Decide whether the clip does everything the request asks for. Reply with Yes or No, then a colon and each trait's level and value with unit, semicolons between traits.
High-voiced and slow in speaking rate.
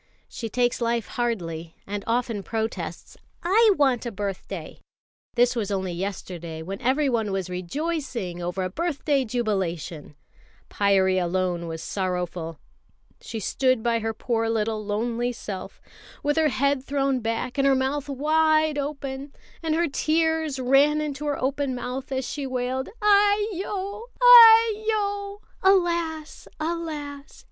Yes: very high, 255 Hz; slow, 130 wpm